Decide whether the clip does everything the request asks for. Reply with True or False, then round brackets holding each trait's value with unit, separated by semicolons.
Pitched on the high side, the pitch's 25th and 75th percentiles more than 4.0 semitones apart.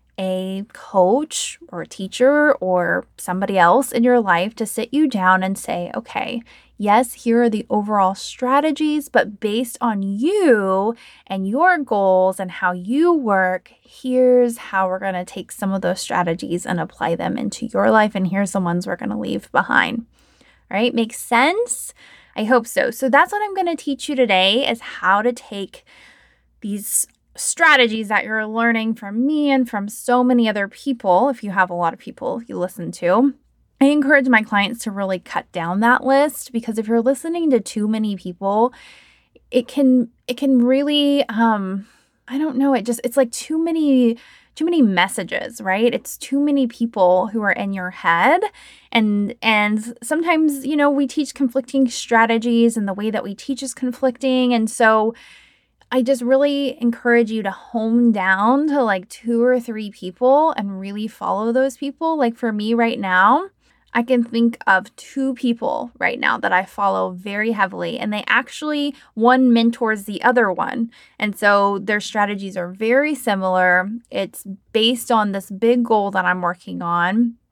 True (230 Hz; 4.7 semitones)